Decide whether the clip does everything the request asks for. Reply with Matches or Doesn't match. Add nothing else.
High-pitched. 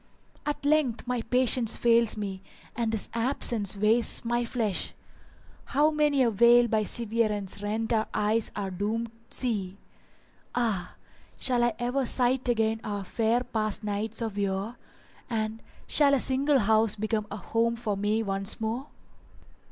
Matches